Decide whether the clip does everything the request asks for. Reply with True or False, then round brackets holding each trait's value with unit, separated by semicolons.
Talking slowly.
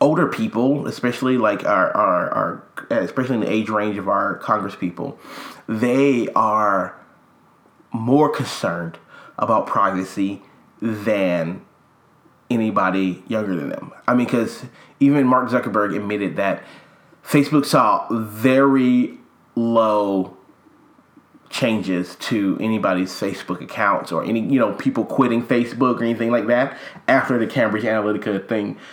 True (125 wpm)